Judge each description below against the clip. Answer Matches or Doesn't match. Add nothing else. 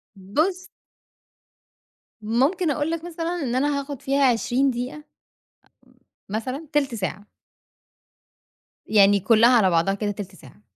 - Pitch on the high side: Matches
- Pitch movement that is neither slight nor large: Doesn't match